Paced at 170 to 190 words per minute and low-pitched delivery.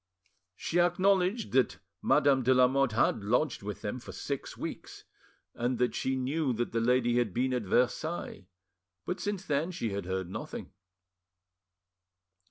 No: average, 145 wpm; low, 130 Hz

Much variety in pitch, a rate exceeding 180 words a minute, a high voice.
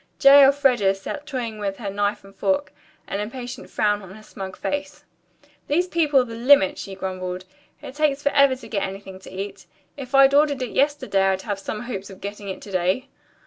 Yes: wide, 6.0 semitones; average, 200 wpm; high, 220 Hz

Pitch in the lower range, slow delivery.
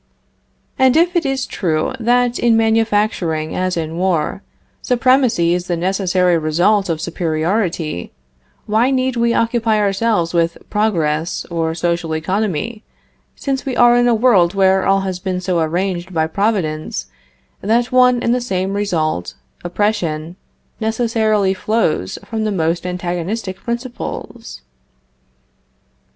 No: high, 195 Hz; slow, 130 wpm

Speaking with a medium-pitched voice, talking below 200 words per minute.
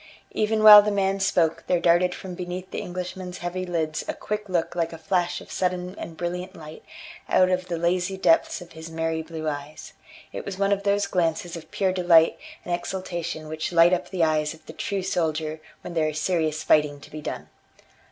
No: medium, 175 Hz; fast, 205 wpm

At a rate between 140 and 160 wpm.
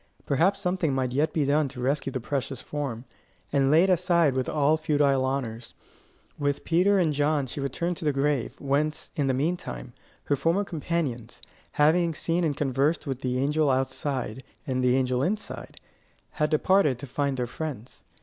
No: average, 180 wpm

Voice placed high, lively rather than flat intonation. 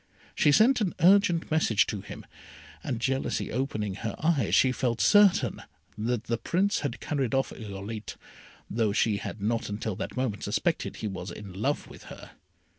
No: low, 120 Hz; wide, 5.9 semitones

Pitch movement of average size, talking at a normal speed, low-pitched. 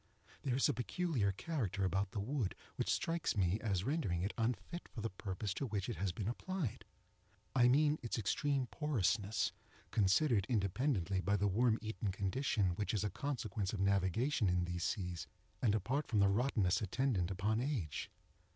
Yes: average, 4.9 semitones; average, 170 wpm; low, 105 Hz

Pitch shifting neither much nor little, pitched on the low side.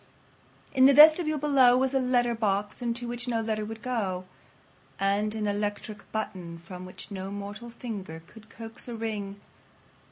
No: average, 3.4 semitones; high, 220 Hz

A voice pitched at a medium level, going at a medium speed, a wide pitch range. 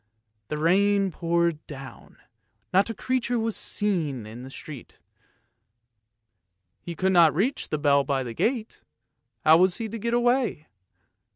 Yes: medium, 175 Hz; average, 155 wpm; wide, 6.8 semitones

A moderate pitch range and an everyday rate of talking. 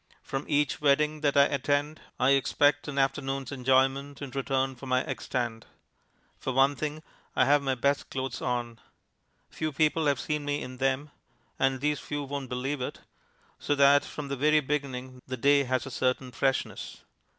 No: narrow, 1.8 semitones; average, 175 wpm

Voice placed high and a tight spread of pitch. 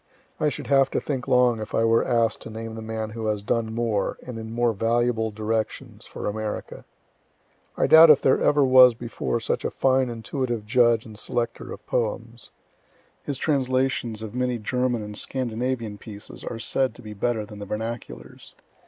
No: low, 115 Hz; narrow, 2.3 semitones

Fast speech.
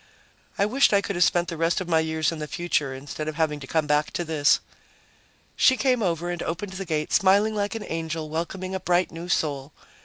Yes: fast, 225 wpm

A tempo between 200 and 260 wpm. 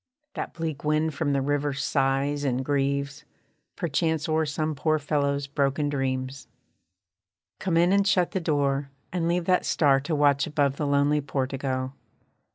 No: average, 155 wpm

